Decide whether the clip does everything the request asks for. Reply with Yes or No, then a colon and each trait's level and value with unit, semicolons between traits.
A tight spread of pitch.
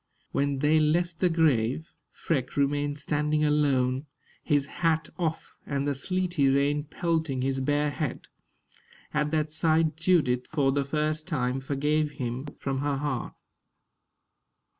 Yes: narrow, 2.3 semitones